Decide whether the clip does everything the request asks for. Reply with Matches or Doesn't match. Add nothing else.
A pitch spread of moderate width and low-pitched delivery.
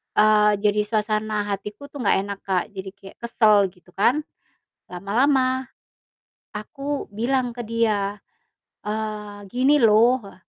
Doesn't match